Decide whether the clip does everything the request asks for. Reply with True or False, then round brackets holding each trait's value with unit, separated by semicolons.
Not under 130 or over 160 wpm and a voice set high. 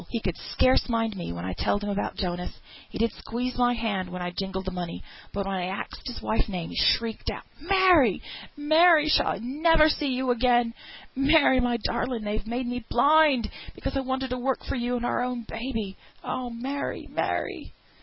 False (200 wpm; 240 Hz)